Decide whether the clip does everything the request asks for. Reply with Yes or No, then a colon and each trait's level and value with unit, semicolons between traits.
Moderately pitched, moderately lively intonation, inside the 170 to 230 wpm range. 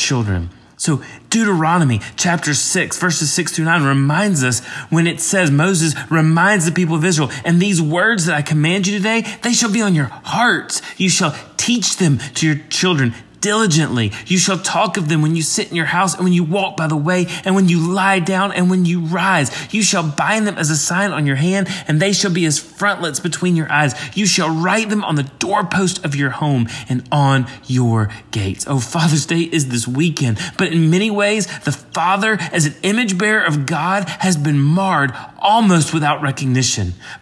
Yes: medium, 165 Hz; average, 4.6 semitones; fast, 205 wpm